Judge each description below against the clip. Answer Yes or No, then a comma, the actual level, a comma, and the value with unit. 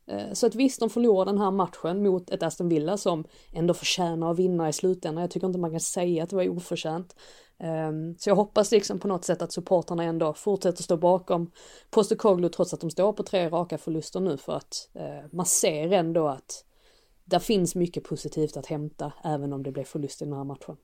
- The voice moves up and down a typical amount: Yes, average, 3.1 semitones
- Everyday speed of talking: No, fast, 215 wpm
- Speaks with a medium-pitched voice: Yes, medium, 175 Hz